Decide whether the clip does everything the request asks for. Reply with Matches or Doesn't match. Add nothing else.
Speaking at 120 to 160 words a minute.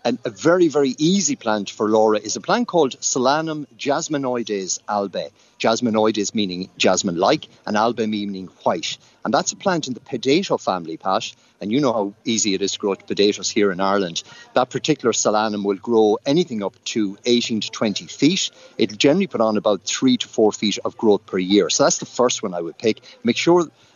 Doesn't match